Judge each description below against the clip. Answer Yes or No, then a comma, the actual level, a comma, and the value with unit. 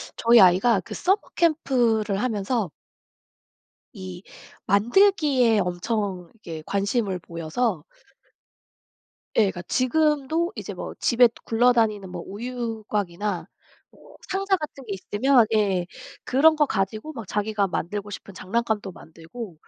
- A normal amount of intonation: Yes, average, 4.6 semitones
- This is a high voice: Yes, high, 215 Hz